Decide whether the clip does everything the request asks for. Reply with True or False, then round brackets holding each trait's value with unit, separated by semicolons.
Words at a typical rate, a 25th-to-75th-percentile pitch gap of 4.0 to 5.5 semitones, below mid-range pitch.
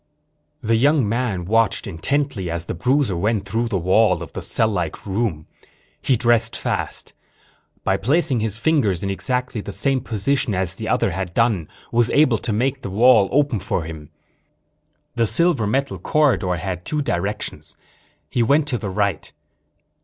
True (165 wpm; 5.1 semitones; 110 Hz)